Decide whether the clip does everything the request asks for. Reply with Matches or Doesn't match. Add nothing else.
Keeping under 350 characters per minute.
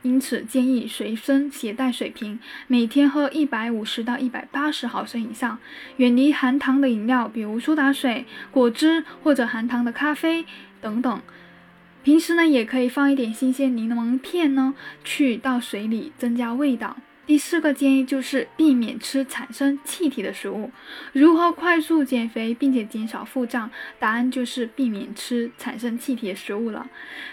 Matches